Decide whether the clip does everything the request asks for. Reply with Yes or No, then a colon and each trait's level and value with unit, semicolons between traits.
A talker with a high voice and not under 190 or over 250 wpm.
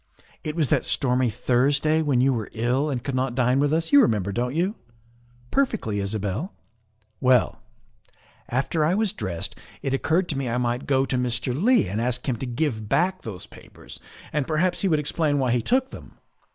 No: low, 130 Hz; average, 195 wpm